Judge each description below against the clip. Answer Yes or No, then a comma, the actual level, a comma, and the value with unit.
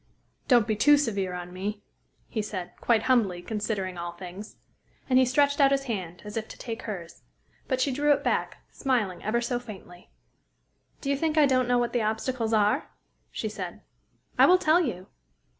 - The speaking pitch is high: Yes, high, 225 Hz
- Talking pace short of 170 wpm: No, average, 190 wpm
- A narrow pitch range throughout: No, average, 5.1 semitones